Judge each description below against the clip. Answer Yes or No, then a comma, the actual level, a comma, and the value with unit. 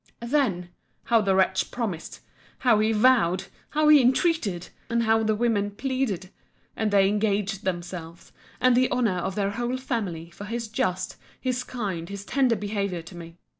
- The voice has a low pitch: No, high, 210 Hz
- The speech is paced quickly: No, average, 145 wpm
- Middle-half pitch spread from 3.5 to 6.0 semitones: Yes, average, 4.4 semitones